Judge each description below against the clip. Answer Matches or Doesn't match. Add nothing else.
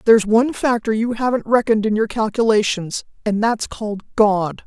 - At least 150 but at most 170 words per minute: Matches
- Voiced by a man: Doesn't match